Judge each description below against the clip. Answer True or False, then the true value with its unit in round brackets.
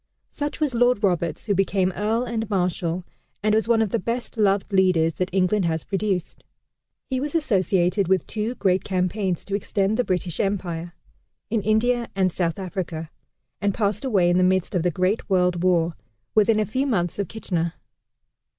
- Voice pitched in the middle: False (195 Hz)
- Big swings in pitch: False (3.3 semitones)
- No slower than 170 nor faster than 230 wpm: True (180 wpm)